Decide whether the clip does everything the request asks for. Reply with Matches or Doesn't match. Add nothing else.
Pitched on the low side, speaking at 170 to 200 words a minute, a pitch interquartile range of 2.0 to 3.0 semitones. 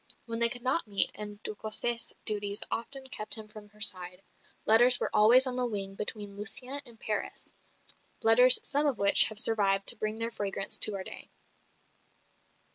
Doesn't match